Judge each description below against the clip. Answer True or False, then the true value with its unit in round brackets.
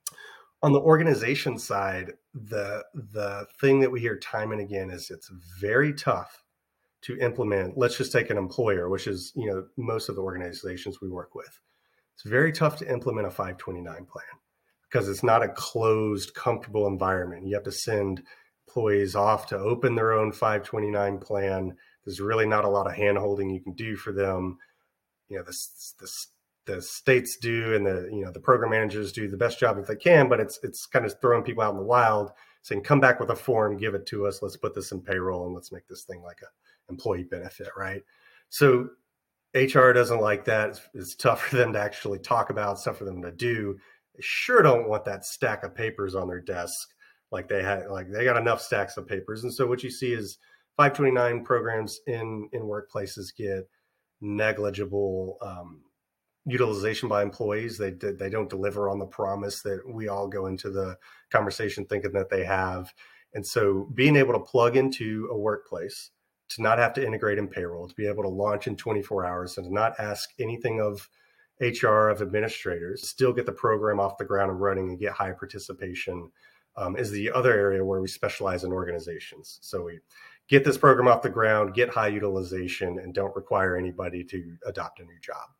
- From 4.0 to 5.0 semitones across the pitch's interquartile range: False (3.3 semitones)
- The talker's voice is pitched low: True (105 Hz)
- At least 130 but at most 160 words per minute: False (200 wpm)